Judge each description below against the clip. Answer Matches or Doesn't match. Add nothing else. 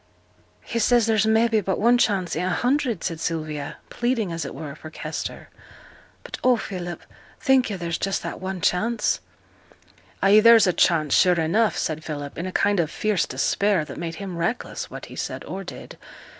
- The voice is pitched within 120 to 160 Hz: Doesn't match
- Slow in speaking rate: Doesn't match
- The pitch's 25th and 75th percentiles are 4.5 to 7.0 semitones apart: Matches